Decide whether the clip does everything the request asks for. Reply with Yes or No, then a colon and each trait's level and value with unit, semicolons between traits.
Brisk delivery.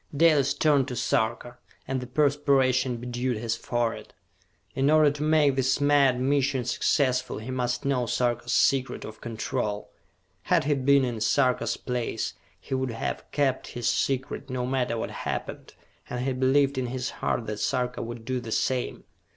No: average, 165 wpm